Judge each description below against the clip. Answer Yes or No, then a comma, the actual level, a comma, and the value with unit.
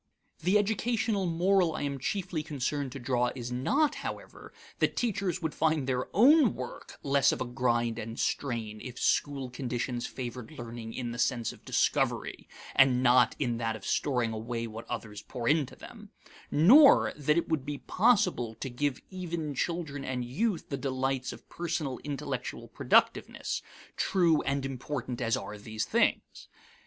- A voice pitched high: No, low, 135 Hz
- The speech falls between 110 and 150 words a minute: No, average, 160 wpm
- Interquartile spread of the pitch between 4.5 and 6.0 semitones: Yes, average, 5.2 semitones